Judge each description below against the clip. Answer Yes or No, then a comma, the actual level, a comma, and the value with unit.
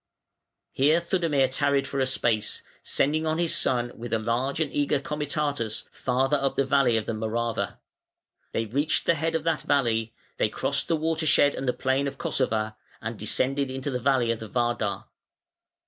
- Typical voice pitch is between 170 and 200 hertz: No, low, 135 Hz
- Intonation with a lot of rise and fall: No, average, 3.9 semitones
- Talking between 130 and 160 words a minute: No, average, 175 wpm